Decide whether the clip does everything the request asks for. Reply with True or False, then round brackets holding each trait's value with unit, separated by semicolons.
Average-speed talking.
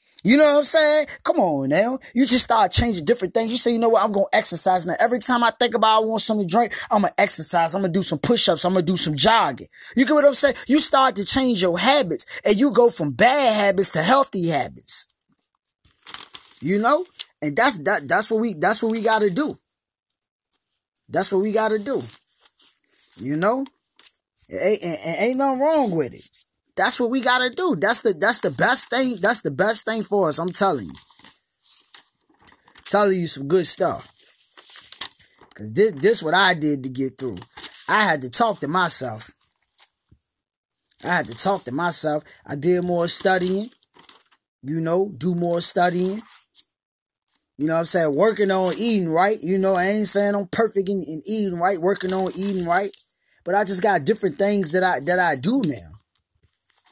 True (195 wpm)